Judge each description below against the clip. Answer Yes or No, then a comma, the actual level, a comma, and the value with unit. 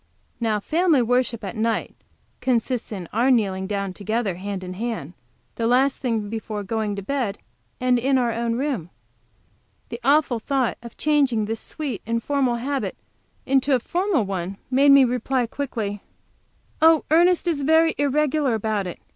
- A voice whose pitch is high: Yes, high, 235 Hz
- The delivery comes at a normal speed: Yes, average, 155 wpm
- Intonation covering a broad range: No, average, 4.5 semitones